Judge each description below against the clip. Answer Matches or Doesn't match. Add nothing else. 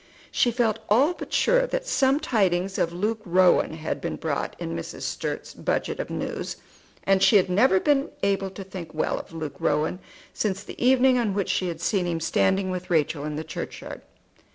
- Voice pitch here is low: Doesn't match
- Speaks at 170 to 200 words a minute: Matches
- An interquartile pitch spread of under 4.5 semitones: Doesn't match